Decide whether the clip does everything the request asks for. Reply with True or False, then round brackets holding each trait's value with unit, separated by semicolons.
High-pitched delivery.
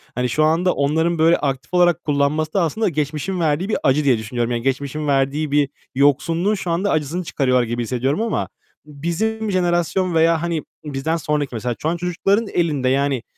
False (155 Hz)